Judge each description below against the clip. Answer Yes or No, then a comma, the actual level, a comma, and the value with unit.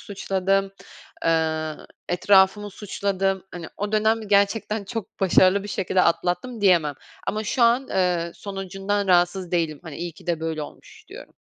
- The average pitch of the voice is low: No, high, 190 Hz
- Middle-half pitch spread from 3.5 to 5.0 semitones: No, average, 2.7 semitones